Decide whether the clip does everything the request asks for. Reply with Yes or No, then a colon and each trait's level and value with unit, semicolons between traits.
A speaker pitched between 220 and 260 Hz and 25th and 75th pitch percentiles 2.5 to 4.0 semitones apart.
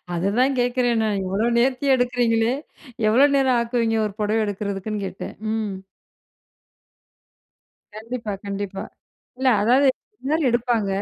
Yes: high, 230 Hz; average, 3.3 semitones